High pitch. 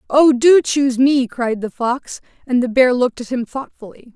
Yes: very high, 255 Hz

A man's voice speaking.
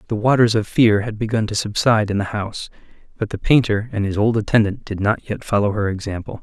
Yes: male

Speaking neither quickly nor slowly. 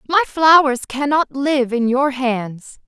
Yes: average, 145 wpm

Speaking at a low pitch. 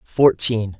Yes: low, 115 Hz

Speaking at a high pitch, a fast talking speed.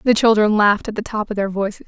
Yes: high, 210 Hz; fast, 290 wpm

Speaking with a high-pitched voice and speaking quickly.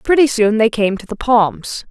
Yes: high, 225 Hz; fast, 220 wpm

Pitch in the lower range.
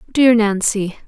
No: high, 220 Hz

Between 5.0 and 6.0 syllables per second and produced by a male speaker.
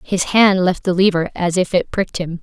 No: 5.3 syllables/s; female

